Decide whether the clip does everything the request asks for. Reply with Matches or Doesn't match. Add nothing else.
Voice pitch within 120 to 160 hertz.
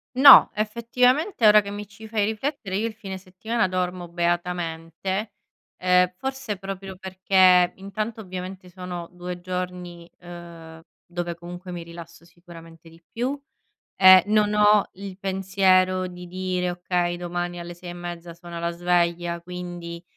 Doesn't match